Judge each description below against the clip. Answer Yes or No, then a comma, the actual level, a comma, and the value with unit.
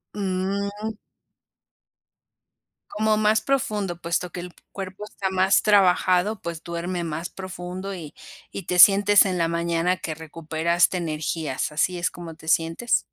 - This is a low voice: No, medium, 180 Hz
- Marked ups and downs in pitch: No, average, 2.8 semitones